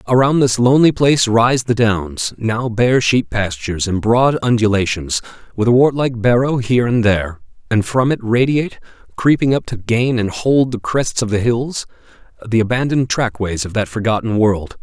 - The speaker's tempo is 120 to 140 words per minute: No, average, 180 wpm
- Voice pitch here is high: No, low, 115 Hz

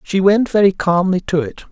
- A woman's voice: No, male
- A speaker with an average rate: No, fast, 210 wpm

